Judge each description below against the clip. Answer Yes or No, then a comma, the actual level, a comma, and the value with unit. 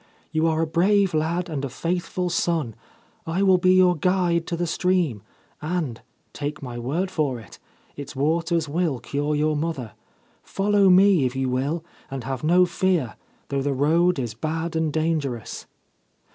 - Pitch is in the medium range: Yes, medium, 160 Hz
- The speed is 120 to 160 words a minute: No, average, 175 wpm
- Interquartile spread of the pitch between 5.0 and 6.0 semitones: No, average, 4.2 semitones